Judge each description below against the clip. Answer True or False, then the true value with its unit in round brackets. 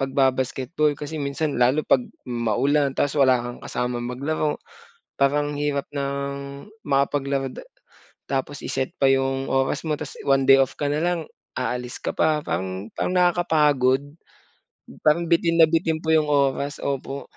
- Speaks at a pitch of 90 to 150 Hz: True (140 Hz)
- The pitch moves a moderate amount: False (2.2 semitones)